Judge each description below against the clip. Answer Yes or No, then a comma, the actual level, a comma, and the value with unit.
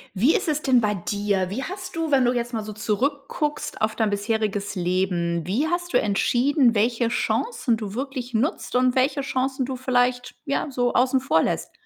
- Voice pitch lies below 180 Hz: No, high, 245 Hz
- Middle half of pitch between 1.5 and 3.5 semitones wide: No, average, 4.5 semitones